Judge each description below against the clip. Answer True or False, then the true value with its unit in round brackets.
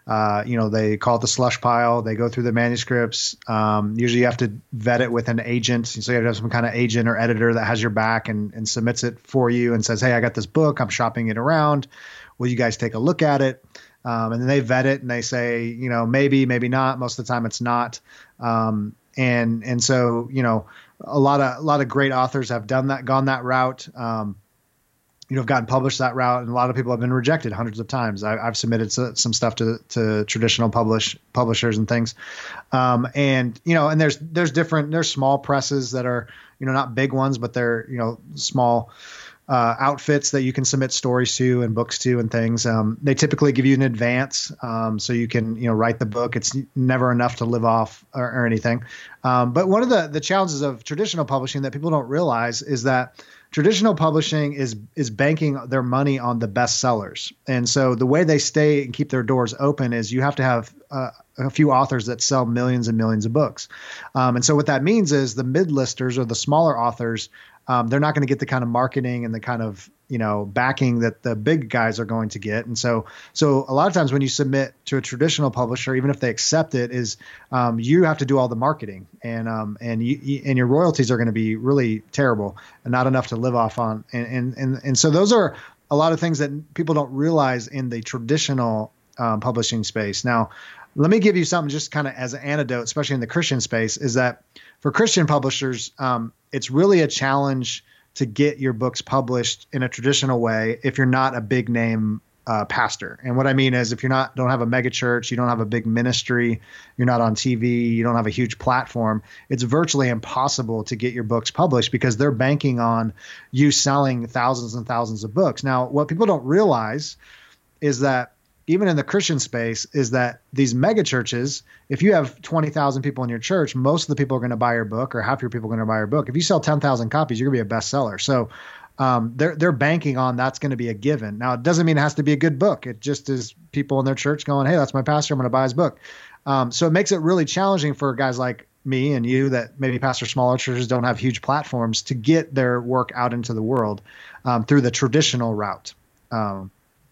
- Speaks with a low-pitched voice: True (125 Hz)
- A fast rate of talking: True (235 wpm)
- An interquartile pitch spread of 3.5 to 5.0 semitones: False (3.0 semitones)